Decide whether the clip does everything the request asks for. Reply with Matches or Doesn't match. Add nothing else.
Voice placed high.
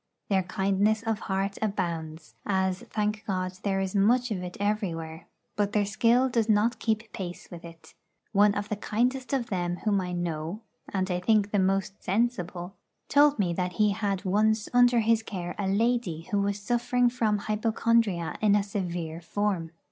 Matches